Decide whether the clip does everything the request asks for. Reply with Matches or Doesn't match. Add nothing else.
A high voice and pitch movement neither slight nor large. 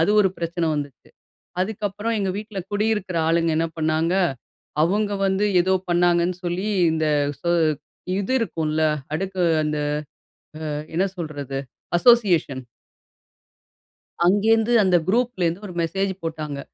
Doesn't match